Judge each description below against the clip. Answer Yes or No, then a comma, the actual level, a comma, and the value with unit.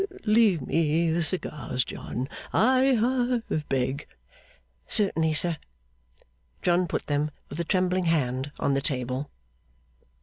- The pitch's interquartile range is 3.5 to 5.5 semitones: Yes, average, 5.1 semitones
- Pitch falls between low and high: Yes, medium, 165 Hz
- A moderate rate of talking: No, slow, 115 wpm